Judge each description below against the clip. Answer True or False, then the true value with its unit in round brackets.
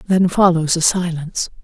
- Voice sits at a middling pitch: True (170 Hz)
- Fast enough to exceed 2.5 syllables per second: True (5.0 syllables/s)